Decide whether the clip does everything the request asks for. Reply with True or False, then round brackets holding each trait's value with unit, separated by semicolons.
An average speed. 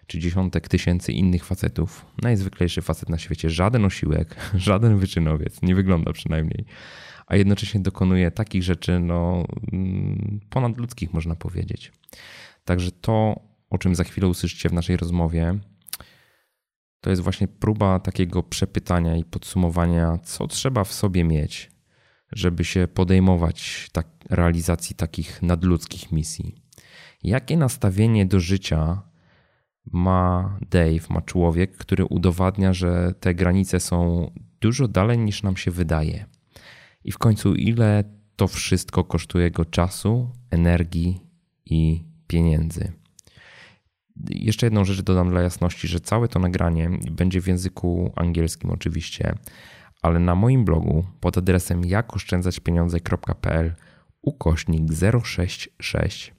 True (120 wpm)